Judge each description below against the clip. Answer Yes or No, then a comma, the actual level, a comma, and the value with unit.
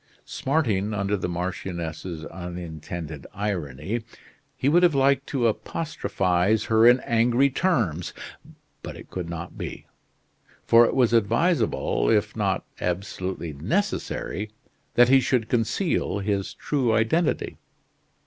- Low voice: Yes, low, 105 Hz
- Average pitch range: No, wide, 5.9 semitones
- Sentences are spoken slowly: Yes, slow, 120 wpm